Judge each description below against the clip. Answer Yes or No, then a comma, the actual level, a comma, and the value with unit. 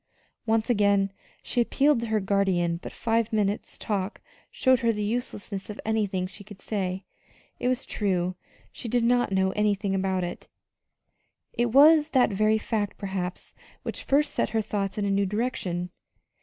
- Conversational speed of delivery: Yes, average, 165 wpm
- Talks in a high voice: Yes, high, 210 Hz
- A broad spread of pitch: No, average, 3.2 semitones